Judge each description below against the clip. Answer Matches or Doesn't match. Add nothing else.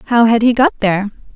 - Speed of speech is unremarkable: Doesn't match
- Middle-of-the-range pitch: Doesn't match